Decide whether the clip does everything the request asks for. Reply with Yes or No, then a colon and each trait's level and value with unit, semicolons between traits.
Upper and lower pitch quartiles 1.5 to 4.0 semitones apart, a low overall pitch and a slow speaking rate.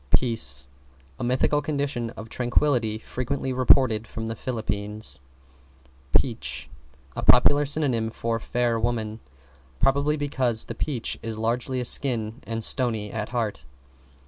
Yes: average, 2.9 semitones; low, 120 Hz; slow, 125 wpm